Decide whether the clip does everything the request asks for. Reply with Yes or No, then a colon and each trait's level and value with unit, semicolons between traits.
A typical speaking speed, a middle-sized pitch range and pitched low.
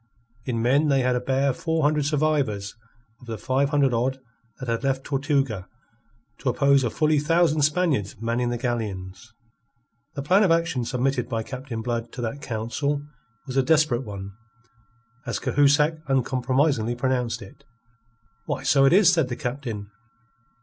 Yes: average, 160 wpm; average, 3.5 semitones; low, 130 Hz